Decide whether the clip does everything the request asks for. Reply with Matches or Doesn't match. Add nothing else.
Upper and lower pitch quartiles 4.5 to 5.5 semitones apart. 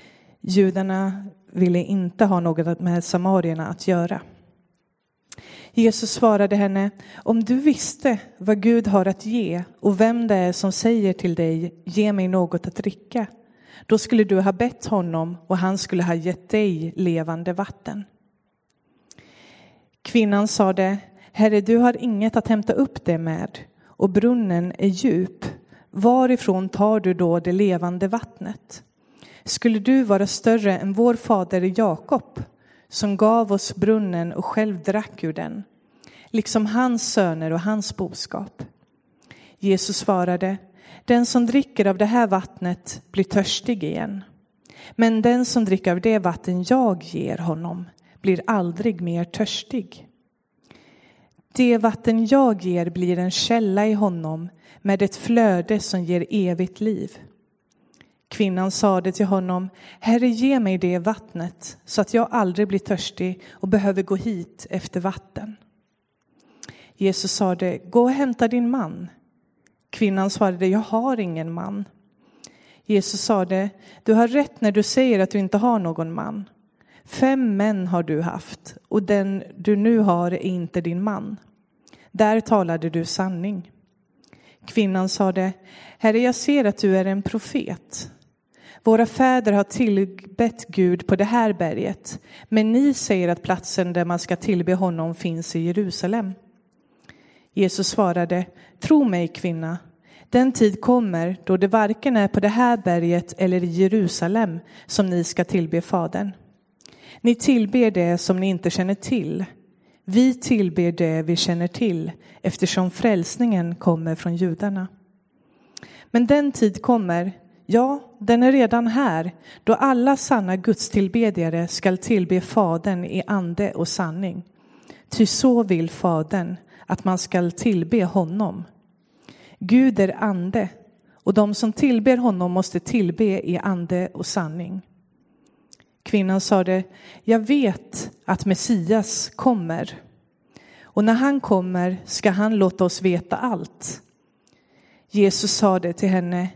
Doesn't match